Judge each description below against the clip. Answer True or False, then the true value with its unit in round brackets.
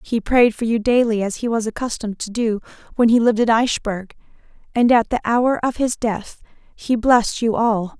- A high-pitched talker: True (230 Hz)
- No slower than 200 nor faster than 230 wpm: True (205 wpm)